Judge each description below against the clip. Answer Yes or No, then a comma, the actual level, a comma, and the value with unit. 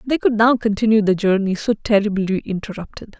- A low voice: No, high, 210 Hz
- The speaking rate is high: No, average, 170 wpm